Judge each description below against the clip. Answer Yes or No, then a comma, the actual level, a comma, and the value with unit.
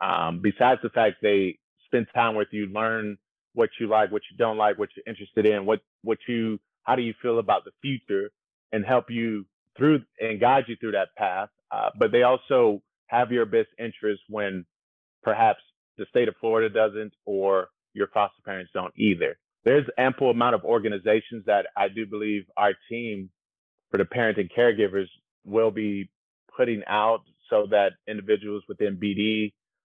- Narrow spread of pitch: Yes, narrow, 2.3 semitones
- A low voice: Yes, low, 110 Hz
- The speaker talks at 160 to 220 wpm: Yes, average, 175 wpm